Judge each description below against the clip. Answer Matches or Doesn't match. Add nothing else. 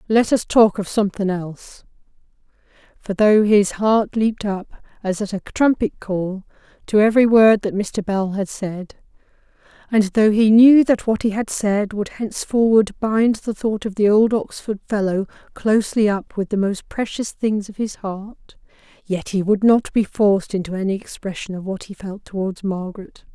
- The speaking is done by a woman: Matches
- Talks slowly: Doesn't match